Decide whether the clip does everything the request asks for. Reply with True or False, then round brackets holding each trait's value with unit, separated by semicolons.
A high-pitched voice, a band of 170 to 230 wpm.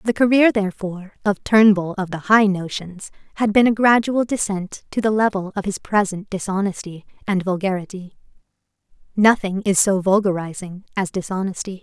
False (195 Hz; 145 wpm)